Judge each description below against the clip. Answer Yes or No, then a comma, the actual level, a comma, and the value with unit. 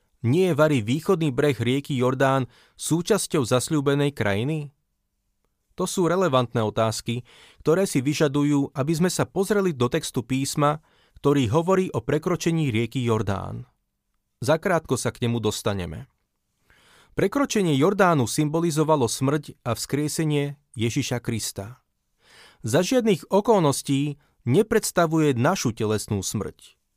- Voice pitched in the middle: Yes, medium, 145 Hz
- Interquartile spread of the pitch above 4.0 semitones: Yes, average, 5.3 semitones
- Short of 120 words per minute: Yes, slow, 110 wpm